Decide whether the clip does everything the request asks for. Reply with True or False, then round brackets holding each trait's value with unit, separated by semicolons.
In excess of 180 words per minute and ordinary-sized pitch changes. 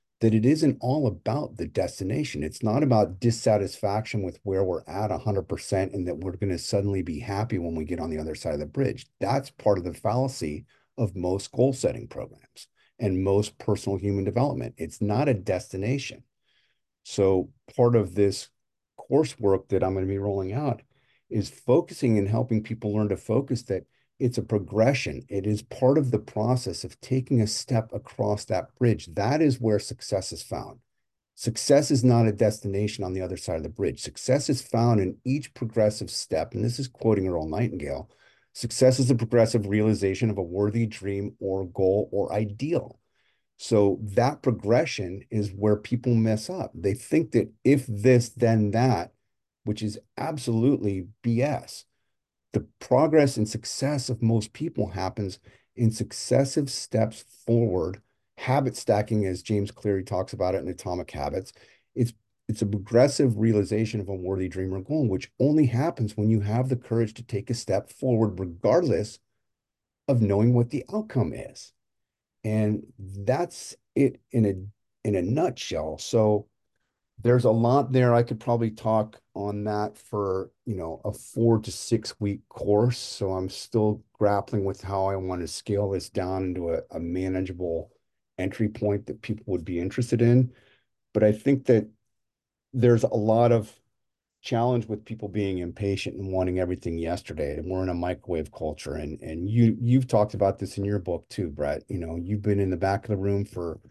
False (175 wpm; 3.6 semitones)